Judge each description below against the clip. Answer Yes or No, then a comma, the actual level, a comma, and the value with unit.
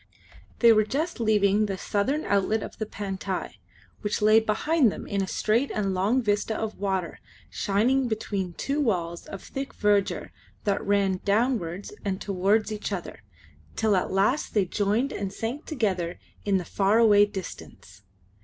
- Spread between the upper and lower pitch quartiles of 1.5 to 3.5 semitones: Yes, narrow, 2.5 semitones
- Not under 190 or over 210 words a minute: No, average, 160 wpm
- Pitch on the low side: No, high, 205 Hz